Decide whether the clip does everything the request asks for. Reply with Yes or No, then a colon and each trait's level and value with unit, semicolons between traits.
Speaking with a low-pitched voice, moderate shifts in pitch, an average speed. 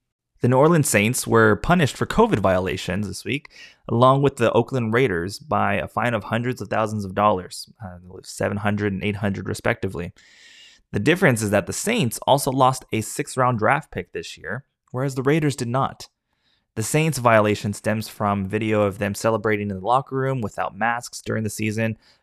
Yes: low, 110 Hz; average, 3.6 semitones; average, 180 wpm